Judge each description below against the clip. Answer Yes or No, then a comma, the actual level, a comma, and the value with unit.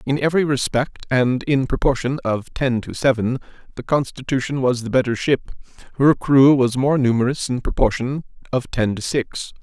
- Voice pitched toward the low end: Yes, low, 130 Hz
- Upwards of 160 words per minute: Yes, average, 170 wpm